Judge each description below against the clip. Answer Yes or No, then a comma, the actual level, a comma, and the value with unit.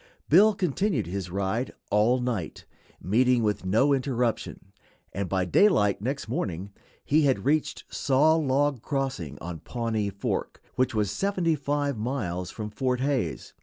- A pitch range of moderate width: No, wide, 5.8 semitones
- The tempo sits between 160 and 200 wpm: No, average, 140 wpm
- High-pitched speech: No, low, 125 Hz